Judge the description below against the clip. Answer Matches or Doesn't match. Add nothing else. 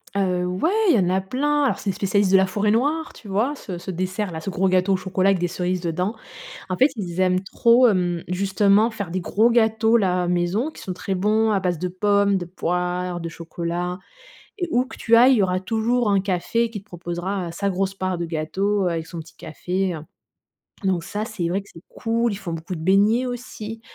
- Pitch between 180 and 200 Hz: Matches